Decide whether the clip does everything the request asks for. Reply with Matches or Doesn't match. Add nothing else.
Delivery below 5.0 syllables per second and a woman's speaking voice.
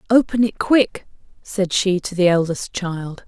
Matches